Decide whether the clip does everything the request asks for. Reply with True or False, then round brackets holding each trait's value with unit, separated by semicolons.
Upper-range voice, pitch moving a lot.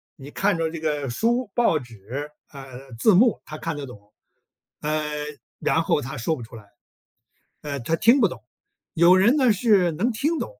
False (160 Hz; 7.3 semitones)